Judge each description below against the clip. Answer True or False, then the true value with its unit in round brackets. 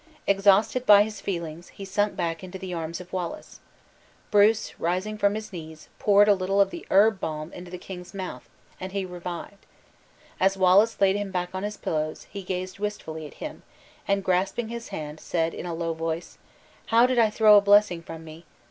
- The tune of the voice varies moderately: True (3.2 semitones)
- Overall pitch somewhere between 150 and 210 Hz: True (190 Hz)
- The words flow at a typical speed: True (195 wpm)